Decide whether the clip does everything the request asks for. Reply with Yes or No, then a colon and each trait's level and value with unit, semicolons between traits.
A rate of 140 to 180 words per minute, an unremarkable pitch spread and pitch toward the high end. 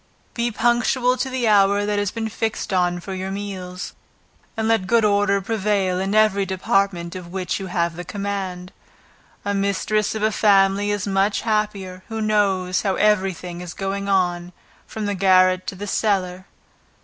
No: average, 175 wpm; narrow, 2.3 semitones; high, 195 Hz